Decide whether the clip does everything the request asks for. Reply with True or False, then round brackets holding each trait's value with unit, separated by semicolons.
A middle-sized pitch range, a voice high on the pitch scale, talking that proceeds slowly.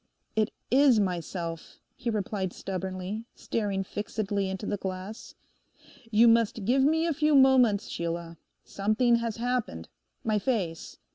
True (3.9 semitones; 210 Hz; 130 wpm)